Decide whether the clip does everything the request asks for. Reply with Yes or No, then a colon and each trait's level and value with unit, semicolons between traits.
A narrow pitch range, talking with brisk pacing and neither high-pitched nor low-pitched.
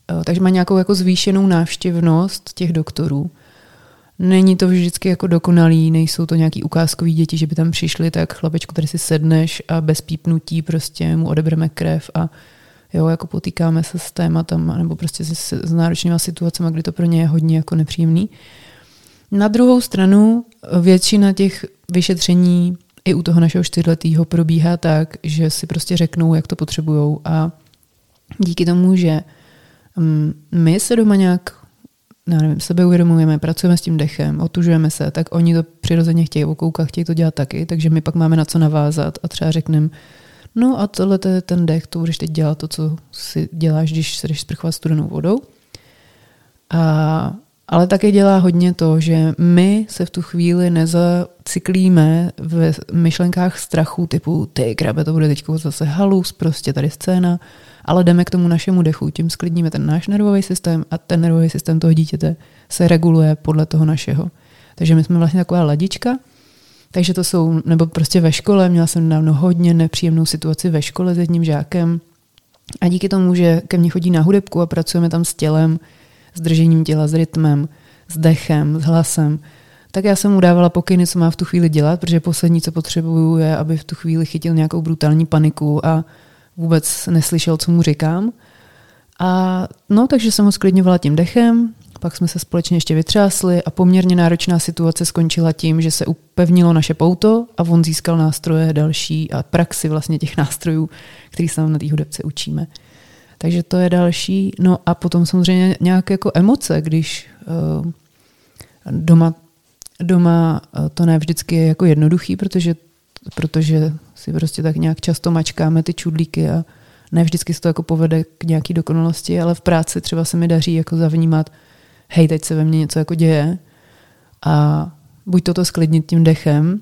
Yes: narrow, 1.8 semitones; fast, 175 wpm; medium, 165 Hz